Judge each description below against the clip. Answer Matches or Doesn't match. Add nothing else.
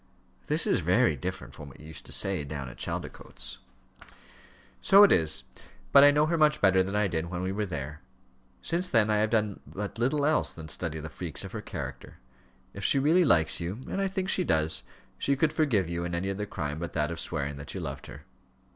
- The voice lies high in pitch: Doesn't match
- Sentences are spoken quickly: Matches